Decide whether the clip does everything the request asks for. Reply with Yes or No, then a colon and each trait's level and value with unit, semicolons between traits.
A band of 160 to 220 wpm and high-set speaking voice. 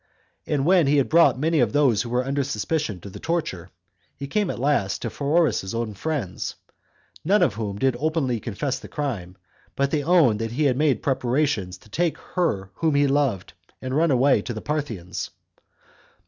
No: average, 190 wpm; low, 135 Hz